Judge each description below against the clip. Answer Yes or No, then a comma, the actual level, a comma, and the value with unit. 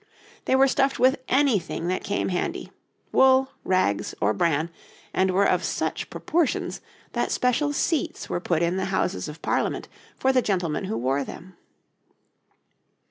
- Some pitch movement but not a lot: No, wide, 7.7 semitones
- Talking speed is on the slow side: No, average, 150 wpm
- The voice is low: No, high, 190 Hz